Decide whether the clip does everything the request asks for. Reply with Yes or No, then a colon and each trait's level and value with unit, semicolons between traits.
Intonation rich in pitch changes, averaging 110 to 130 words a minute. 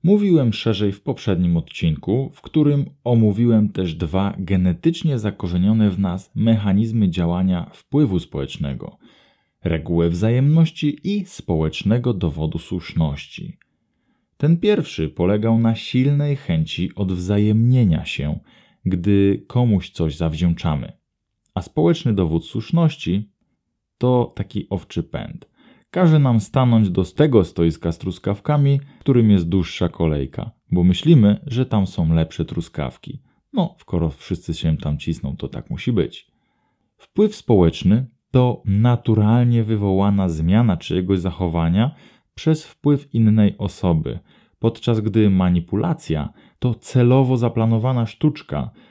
Yes: wide, 5.8 semitones; average, 115 wpm